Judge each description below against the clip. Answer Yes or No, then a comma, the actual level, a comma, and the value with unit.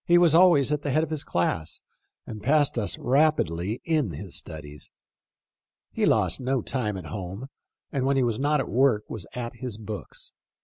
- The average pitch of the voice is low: Yes, low, 125 Hz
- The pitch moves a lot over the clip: Yes, wide, 6.1 semitones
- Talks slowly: No, average, 185 wpm